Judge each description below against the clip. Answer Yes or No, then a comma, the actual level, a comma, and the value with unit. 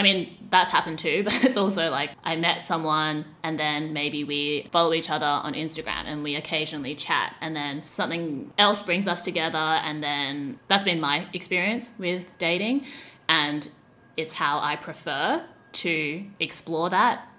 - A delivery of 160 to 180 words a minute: Yes, average, 165 wpm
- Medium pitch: Yes, medium, 160 Hz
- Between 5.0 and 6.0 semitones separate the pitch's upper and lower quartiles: No, average, 3.4 semitones